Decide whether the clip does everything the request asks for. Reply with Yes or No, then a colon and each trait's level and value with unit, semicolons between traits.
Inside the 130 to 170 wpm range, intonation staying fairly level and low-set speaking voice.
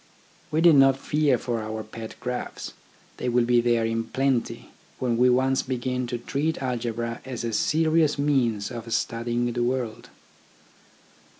Yes: average, 155 wpm; narrow, 2.3 semitones; low, 125 Hz